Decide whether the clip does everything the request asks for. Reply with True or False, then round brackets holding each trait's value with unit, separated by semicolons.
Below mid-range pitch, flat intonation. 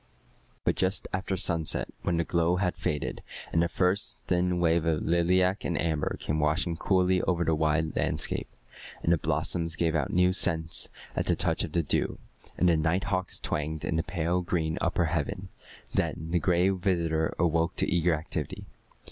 True (85 Hz; 2.1 semitones)